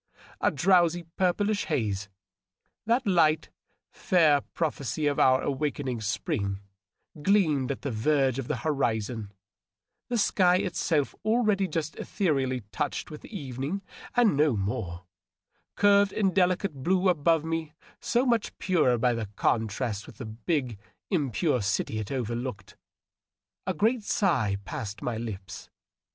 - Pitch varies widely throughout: Yes, wide, 7.7 semitones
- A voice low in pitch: No, medium, 145 Hz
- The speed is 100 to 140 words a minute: Yes, slow, 135 wpm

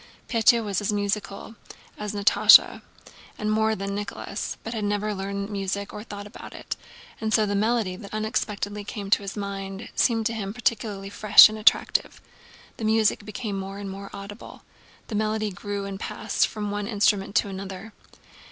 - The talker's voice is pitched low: No, high, 205 Hz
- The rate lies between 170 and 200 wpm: Yes, average, 175 wpm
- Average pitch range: No, narrow, 1.5 semitones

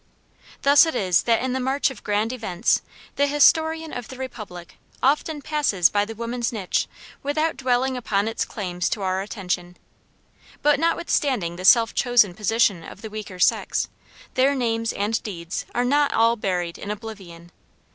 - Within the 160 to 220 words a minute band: Yes, average, 165 wpm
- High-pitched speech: Yes, high, 225 Hz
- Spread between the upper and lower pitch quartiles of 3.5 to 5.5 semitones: Yes, average, 5.2 semitones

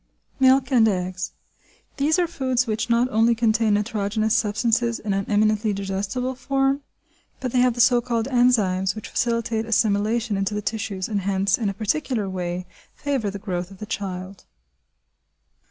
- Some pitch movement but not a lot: Yes, average, 3.5 semitones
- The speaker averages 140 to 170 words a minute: Yes, average, 160 wpm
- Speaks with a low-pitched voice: No, high, 220 Hz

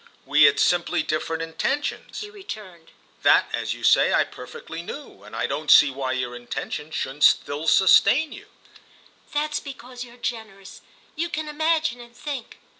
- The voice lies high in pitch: Yes, high, 220 Hz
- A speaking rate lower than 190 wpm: Yes, average, 155 wpm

